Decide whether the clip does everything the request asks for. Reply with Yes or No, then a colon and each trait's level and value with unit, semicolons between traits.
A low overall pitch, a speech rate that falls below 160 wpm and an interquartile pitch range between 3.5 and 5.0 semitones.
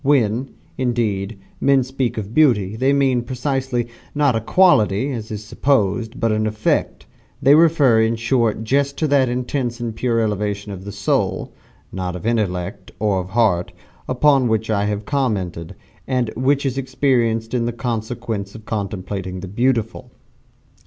Yes: low, 115 Hz; average, 150 wpm; average, 4.0 semitones